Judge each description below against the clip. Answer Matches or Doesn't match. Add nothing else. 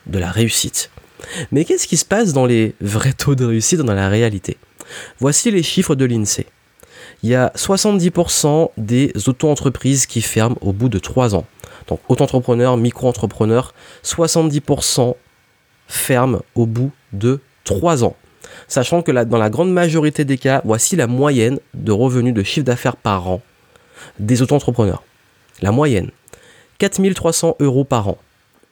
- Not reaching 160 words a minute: Matches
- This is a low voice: Matches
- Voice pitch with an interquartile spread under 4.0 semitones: Doesn't match